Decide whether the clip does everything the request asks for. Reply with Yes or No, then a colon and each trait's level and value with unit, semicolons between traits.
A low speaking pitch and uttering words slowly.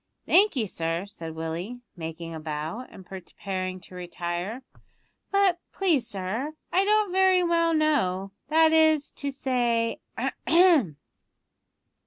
No: high, 235 Hz; slow, 125 wpm